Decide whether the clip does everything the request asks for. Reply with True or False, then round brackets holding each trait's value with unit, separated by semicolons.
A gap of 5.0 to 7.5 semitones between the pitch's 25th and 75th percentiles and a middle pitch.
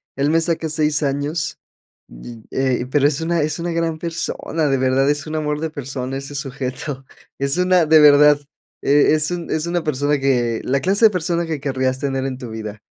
False (3.1 semitones; 145 Hz)